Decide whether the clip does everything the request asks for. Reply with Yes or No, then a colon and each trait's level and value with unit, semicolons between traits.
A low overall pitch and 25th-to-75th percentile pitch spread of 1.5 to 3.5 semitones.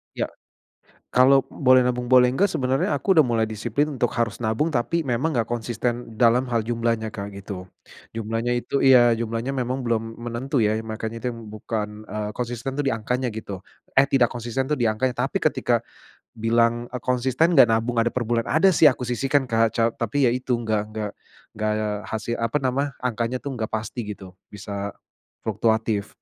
Yes: low, 120 Hz; narrow, 2.4 semitones